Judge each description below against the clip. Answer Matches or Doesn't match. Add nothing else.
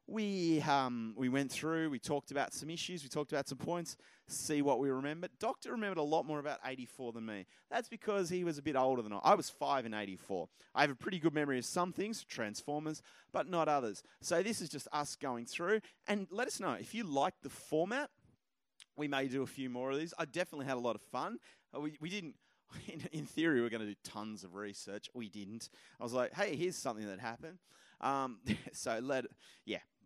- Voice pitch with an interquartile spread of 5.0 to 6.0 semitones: Matches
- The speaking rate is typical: Doesn't match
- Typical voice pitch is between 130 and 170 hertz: Matches